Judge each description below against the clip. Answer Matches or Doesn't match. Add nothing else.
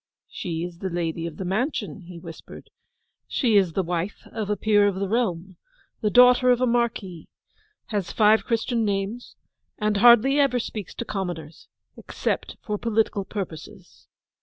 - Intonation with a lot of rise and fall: Doesn't match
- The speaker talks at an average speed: Matches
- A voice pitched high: Matches